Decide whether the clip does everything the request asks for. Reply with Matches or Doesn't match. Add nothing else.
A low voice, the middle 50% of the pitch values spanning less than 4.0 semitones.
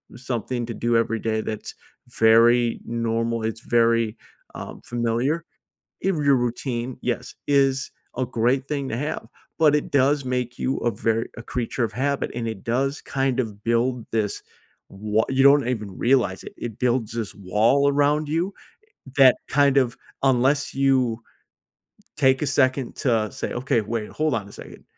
Matches